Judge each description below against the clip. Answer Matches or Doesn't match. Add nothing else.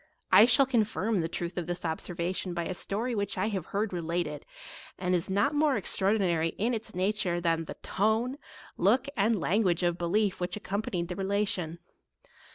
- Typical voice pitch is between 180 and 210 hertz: Matches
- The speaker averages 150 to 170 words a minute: Doesn't match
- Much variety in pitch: Doesn't match